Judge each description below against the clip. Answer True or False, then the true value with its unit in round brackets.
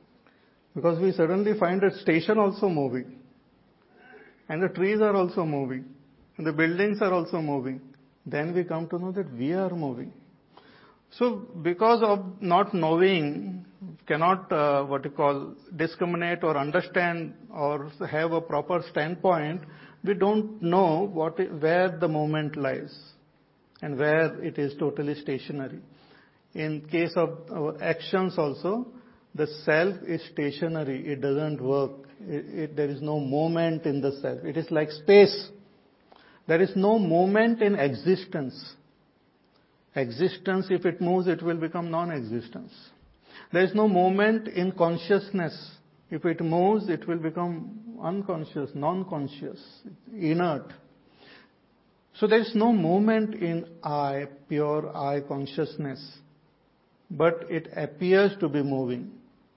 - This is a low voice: False (165 Hz)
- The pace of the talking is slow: True (130 wpm)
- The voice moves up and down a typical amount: True (4.2 semitones)